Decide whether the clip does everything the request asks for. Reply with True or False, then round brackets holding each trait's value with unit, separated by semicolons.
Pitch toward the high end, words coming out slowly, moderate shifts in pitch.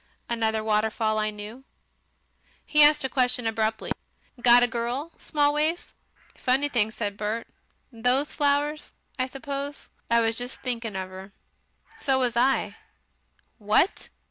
True (240 Hz; 130 wpm; 4.1 semitones)